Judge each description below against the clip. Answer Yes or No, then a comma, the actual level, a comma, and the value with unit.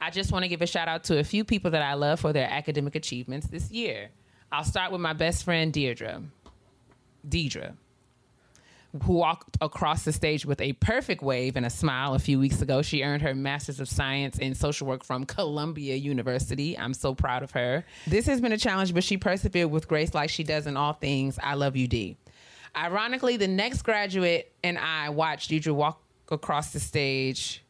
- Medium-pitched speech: Yes, medium, 145 Hz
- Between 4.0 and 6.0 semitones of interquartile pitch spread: No, average, 3.6 semitones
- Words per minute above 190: Yes, fast, 205 wpm